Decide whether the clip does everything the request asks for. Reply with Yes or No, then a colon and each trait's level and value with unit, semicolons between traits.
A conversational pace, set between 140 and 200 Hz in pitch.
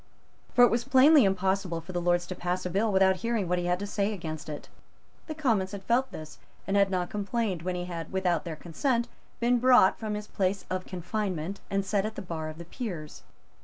No: fast, 225 wpm; high, 190 Hz